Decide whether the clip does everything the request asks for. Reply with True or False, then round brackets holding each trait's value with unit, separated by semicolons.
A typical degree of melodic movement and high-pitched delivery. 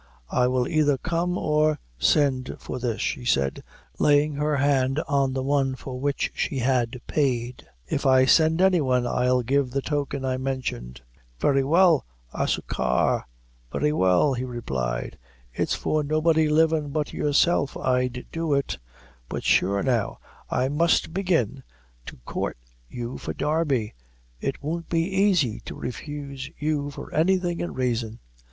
False (3.4 semitones; 140 Hz)